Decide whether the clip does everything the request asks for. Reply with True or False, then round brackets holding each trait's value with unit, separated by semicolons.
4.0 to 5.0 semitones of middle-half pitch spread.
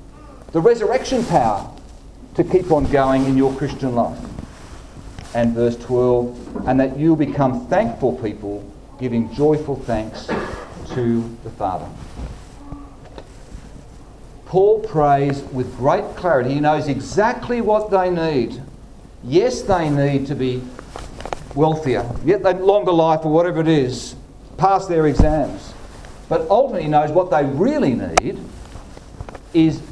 True (4.5 semitones)